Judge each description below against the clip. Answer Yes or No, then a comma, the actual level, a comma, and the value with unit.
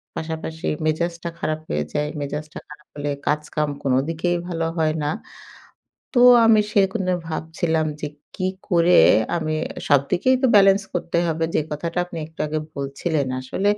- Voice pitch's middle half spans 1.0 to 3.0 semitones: Yes, narrow, 2.6 semitones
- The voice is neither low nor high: Yes, medium, 160 Hz